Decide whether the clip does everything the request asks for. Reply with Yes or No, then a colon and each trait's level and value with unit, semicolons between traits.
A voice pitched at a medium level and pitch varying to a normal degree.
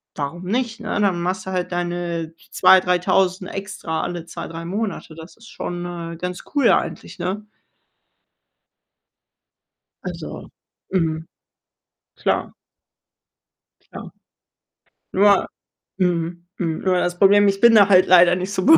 No: medium, 180 Hz; narrow, 2.3 semitones